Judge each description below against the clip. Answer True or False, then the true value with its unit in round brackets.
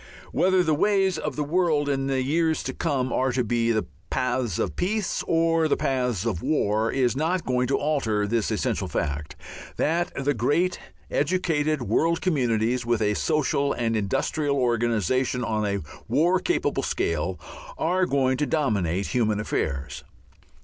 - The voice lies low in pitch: True (130 Hz)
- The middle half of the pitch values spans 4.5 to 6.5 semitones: True (5.4 semitones)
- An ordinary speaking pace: True (155 wpm)